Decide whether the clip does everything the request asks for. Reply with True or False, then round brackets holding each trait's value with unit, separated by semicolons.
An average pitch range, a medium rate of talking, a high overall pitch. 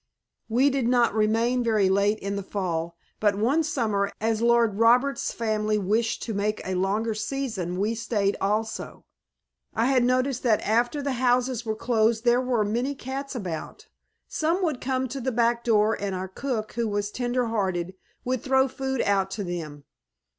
True (3.6 semitones; 175 wpm; 225 Hz)